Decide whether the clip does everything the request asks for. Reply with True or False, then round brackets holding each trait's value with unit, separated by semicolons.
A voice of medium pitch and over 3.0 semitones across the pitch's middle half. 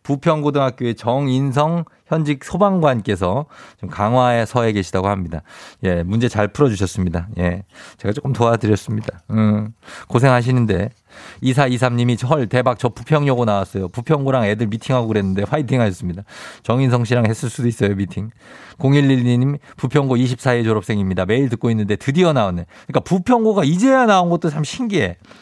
False (120 Hz; 5.2 semitones)